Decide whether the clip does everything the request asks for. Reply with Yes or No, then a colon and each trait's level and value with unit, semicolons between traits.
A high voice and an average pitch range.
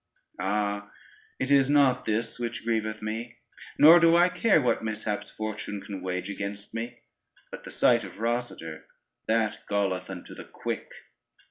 No: low, 110 Hz; average, 3.1 semitones